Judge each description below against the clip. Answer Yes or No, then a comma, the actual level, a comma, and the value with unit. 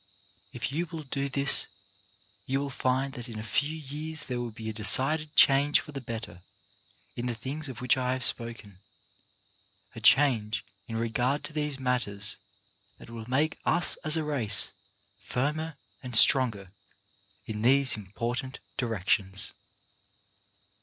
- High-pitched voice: No, low, 125 Hz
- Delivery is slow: No, average, 150 wpm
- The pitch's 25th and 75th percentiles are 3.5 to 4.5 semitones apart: Yes, average, 4.2 semitones